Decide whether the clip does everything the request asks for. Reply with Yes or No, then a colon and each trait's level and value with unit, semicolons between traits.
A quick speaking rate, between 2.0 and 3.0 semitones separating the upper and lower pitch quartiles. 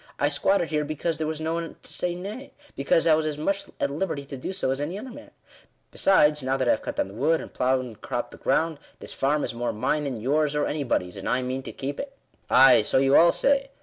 No: fast, 270 wpm; average, 3.8 semitones